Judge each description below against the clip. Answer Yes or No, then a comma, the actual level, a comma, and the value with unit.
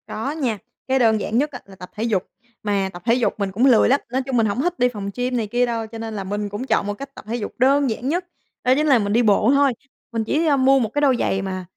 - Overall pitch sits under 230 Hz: No, high, 235 Hz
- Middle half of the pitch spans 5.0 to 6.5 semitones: No, average, 4.3 semitones